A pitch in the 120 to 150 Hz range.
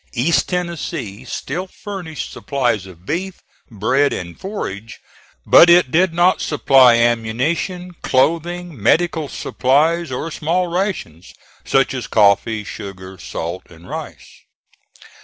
Yes: medium, 140 Hz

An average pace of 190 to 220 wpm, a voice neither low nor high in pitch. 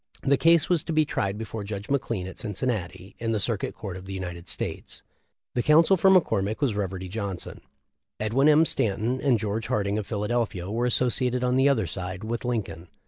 No: average, 195 wpm; low, 110 Hz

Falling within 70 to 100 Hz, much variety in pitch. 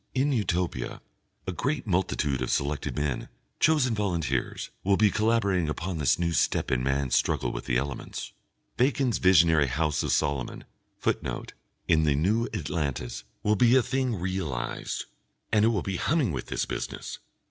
Yes: very low, 85 Hz; wide, 7.3 semitones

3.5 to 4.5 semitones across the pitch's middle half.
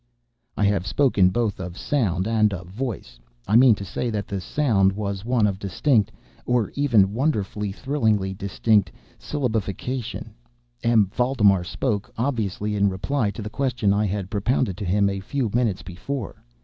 Yes: average, 3.9 semitones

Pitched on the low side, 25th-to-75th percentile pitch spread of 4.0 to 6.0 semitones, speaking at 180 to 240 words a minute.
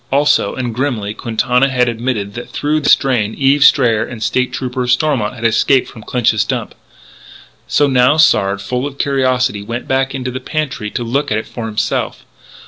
No: low, 125 Hz; average, 3.1 semitones; average, 185 wpm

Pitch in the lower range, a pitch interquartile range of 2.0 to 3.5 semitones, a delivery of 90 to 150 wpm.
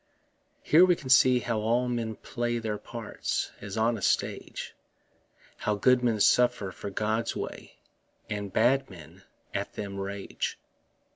Yes: low, 115 Hz; average, 3.1 semitones; average, 145 wpm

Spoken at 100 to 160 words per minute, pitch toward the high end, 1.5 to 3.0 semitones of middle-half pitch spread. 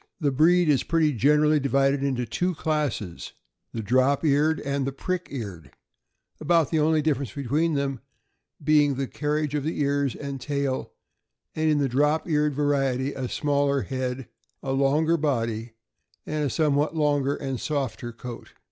No: average, 155 wpm; medium, 140 Hz; narrow, 2.4 semitones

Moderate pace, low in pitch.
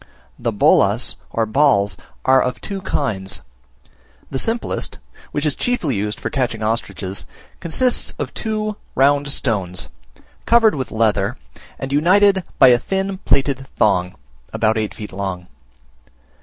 No: slow, 130 wpm; low, 130 Hz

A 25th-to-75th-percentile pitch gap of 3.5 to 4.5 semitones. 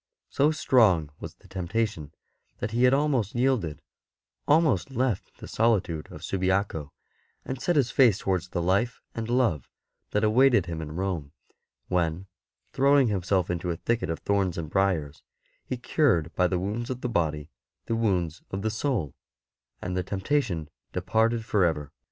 No: wide, 5.6 semitones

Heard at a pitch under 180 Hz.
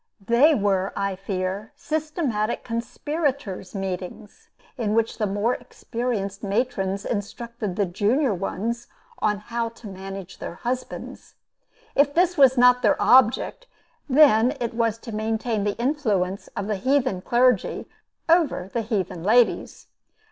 No: high, 225 Hz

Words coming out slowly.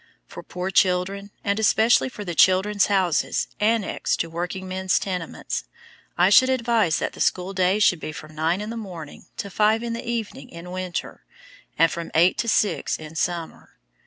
No: average, 175 wpm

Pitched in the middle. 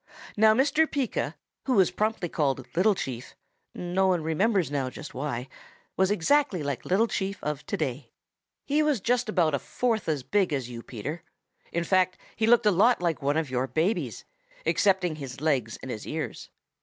Yes: medium, 175 Hz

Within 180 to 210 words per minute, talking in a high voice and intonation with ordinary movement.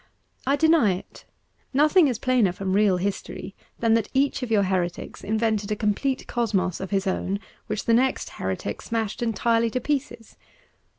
No: average, 165 wpm; high, 225 Hz; average, 4.2 semitones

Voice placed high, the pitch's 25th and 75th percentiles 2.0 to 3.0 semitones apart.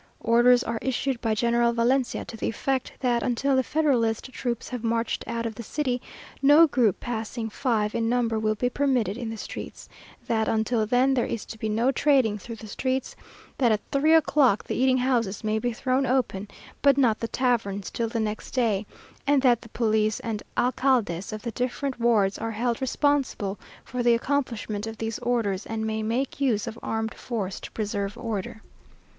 Yes: high, 235 Hz; average, 2.7 semitones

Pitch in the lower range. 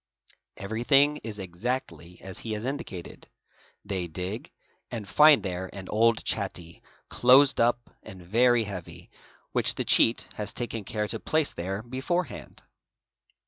Yes: low, 110 Hz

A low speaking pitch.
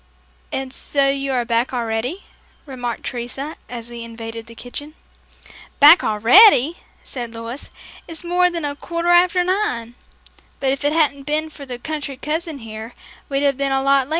No: very high, 275 Hz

